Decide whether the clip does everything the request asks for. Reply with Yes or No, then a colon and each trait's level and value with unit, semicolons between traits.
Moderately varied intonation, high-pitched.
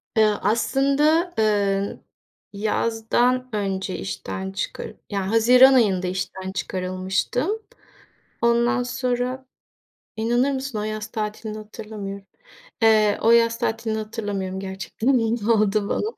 Yes: average, 3.5 semitones; high, 220 Hz